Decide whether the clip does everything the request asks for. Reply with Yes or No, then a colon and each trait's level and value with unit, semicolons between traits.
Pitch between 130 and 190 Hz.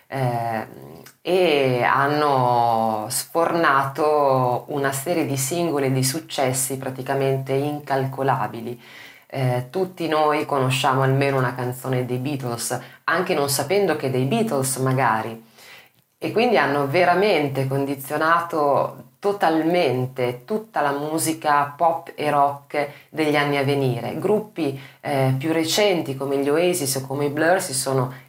Yes: medium, 140 Hz